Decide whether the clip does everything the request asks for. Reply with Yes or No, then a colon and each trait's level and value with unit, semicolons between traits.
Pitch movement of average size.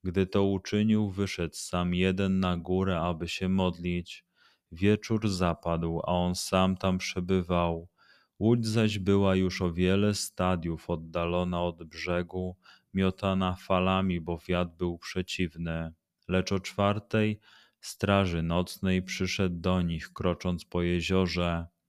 No: narrow, 1.7 semitones